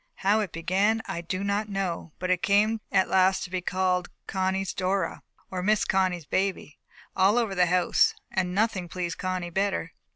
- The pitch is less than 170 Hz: No, medium, 185 Hz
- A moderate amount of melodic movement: No, narrow, 1.7 semitones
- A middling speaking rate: Yes, average, 175 wpm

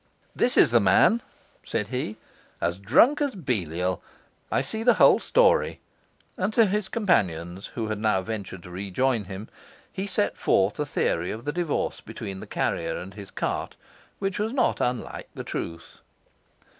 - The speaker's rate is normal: Yes, average, 170 wpm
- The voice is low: Yes, low, 110 Hz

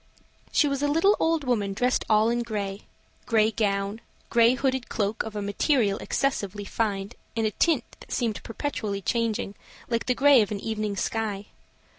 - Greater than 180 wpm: No, average, 170 wpm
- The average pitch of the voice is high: Yes, high, 220 Hz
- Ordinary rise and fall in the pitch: Yes, average, 3.7 semitones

